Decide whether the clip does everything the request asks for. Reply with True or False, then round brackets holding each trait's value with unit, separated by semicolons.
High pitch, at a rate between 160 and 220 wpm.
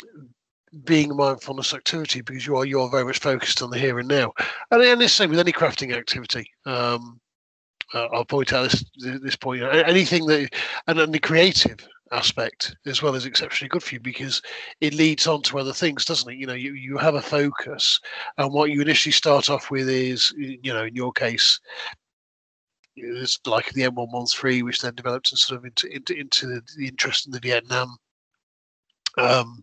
False (135 Hz; 205 wpm)